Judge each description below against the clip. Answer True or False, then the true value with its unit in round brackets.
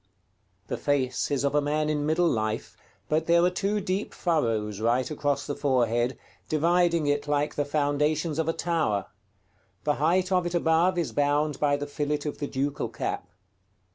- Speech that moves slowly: False (175 wpm)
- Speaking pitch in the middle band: True (150 Hz)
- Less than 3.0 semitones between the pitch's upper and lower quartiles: True (2.5 semitones)